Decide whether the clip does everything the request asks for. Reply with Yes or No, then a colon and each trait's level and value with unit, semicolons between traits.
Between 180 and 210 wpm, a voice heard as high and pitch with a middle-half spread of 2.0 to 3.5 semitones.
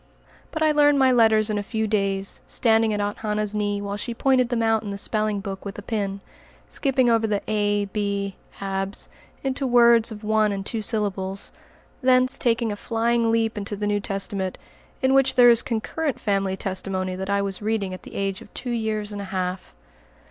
Yes: average, 200 wpm; high, 210 Hz; average, 2.7 semitones